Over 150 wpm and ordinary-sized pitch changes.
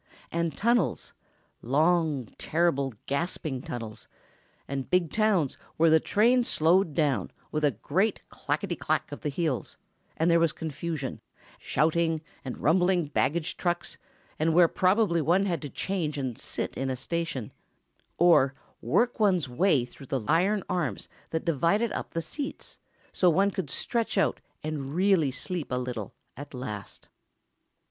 No: average, 140 wpm; average, 4.7 semitones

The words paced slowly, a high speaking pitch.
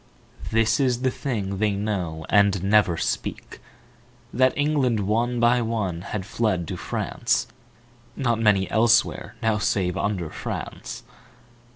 No: slow, 130 wpm; low, 110 Hz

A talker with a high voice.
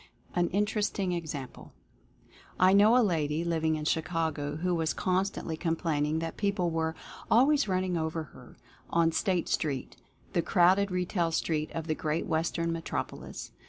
No: medium, 165 Hz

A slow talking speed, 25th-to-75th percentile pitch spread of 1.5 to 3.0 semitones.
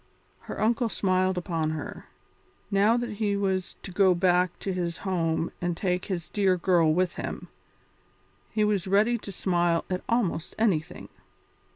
No: average, 155 wpm; average, 2.7 semitones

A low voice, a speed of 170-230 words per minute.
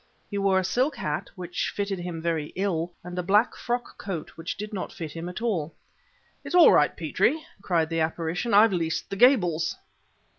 No: medium, 180 Hz; average, 190 wpm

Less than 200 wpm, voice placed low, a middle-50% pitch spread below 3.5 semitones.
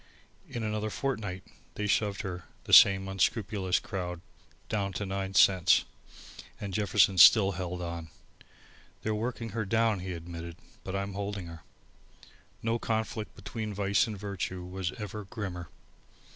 Yes: average, 140 wpm; low, 100 Hz; average, 2.8 semitones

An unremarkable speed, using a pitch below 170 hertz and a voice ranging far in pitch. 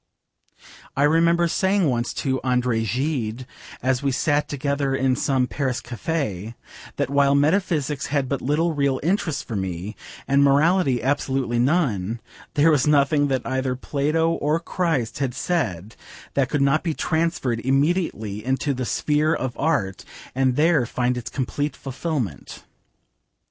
No: average, 145 wpm; medium, 140 Hz; average, 3.5 semitones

